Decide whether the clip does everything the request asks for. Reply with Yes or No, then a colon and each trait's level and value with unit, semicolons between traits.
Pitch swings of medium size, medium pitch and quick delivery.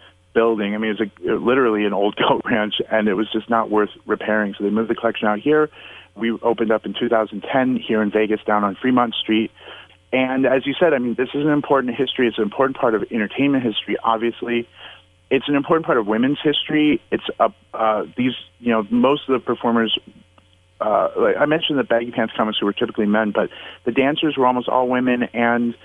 No: average, 3.2 semitones; low, 115 Hz; fast, 220 wpm